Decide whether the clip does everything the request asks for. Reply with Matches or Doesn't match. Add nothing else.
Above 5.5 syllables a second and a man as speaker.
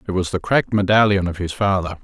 Matches